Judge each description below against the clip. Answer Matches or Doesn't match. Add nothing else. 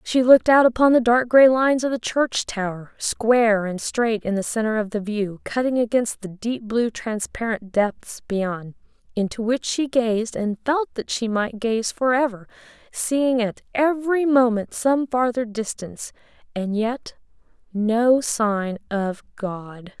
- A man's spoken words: Doesn't match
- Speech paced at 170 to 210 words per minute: Doesn't match